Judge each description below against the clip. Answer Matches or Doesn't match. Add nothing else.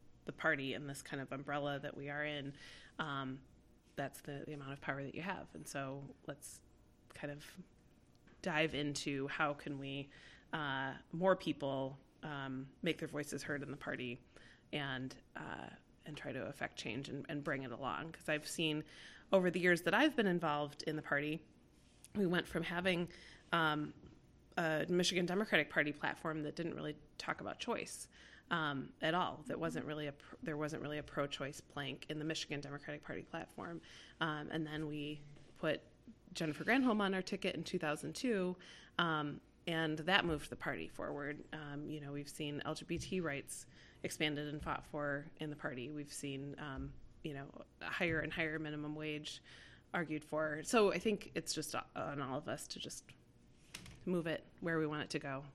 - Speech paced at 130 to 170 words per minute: Doesn't match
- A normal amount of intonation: Doesn't match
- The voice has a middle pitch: Matches